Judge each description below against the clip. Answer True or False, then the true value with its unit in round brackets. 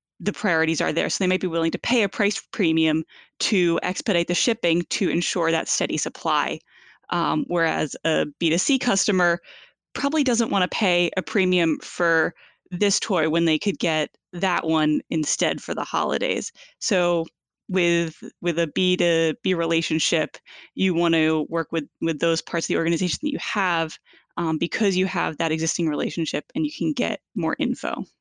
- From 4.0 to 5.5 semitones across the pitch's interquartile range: False (2.7 semitones)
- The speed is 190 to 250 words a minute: False (170 wpm)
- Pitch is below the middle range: False (170 Hz)